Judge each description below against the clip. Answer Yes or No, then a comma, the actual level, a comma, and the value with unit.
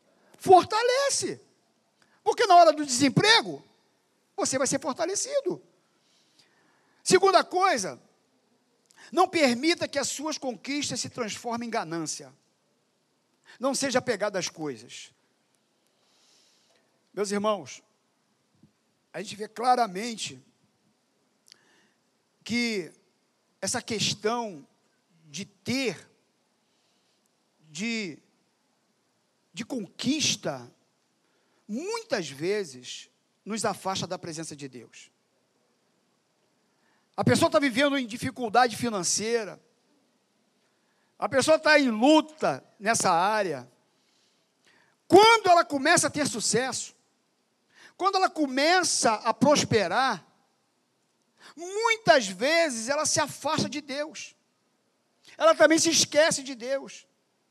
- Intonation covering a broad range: Yes, wide, 6.9 semitones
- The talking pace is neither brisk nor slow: No, slow, 90 wpm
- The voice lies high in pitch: Yes, very high, 260 Hz